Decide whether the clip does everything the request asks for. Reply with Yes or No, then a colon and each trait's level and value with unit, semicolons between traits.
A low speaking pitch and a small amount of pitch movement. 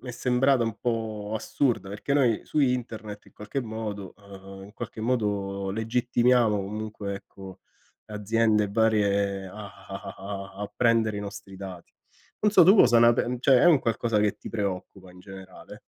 No: low, 110 Hz; average, 3.1 semitones